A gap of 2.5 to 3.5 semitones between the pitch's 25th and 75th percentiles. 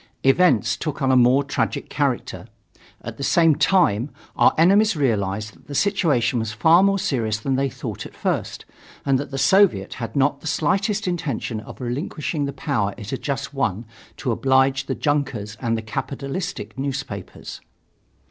No: wide, 5.4 semitones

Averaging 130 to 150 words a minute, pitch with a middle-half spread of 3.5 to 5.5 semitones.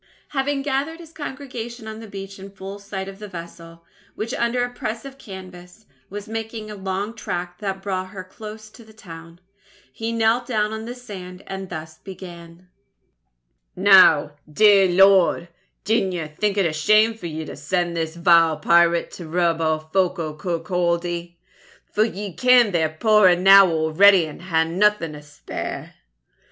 No: average, 165 wpm; average, 4.1 semitones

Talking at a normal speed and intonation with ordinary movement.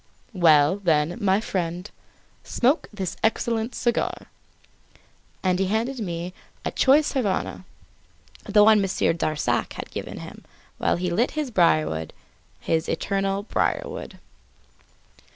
No: slow, 115 wpm; average, 4.8 semitones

